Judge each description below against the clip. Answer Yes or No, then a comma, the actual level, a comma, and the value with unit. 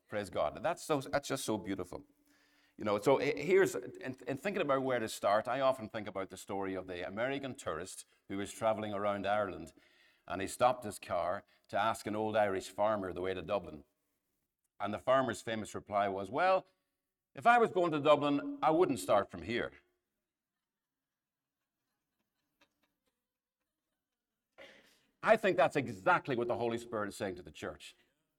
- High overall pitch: No, low, 110 Hz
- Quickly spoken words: No, average, 170 wpm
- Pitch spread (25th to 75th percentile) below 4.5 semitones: No, average, 5.3 semitones